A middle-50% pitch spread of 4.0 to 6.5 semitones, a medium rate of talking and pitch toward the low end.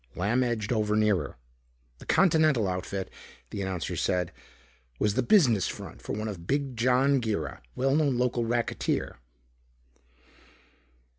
No: average, 4.6 semitones; slow, 125 wpm; low, 115 Hz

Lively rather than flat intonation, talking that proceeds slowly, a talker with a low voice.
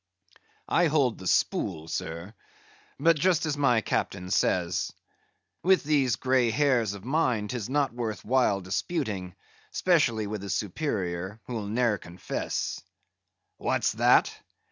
Yes: wide, 6.4 semitones; slow, 125 wpm; low, 115 Hz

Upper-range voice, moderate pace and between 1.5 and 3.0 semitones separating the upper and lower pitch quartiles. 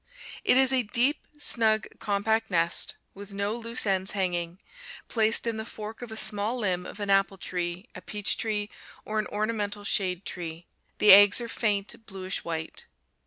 Yes: high, 205 Hz; average, 170 wpm; average, 2.7 semitones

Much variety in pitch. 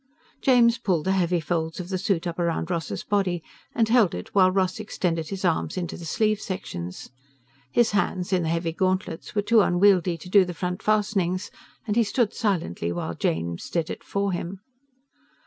No: average, 3.3 semitones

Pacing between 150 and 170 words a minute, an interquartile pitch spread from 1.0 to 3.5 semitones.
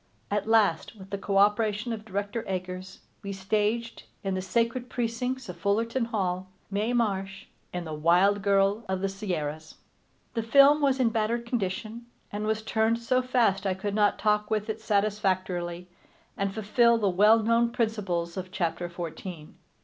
Yes: average, 160 wpm; average, 3.2 semitones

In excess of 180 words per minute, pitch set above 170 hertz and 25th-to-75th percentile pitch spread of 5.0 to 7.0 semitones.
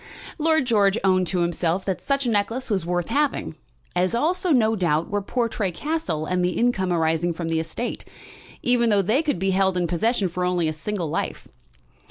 Yes: average, 195 wpm; high, 190 Hz; average, 5.3 semitones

